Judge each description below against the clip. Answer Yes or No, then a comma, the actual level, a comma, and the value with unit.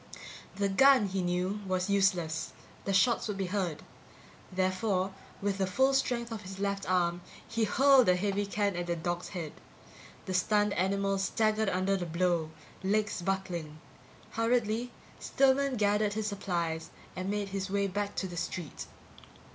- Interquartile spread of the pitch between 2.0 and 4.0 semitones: Yes, narrow, 2.5 semitones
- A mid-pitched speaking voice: No, high, 195 Hz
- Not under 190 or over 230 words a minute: No, average, 155 wpm